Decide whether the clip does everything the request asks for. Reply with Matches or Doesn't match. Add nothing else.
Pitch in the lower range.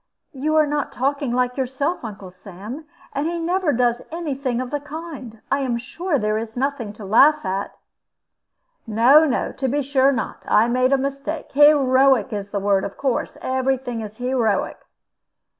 Doesn't match